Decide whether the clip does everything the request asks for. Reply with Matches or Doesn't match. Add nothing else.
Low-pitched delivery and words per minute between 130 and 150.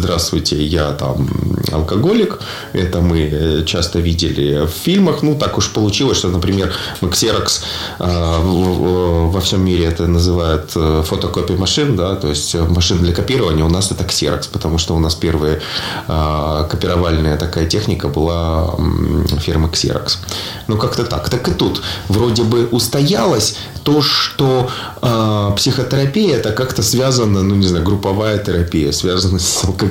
Matches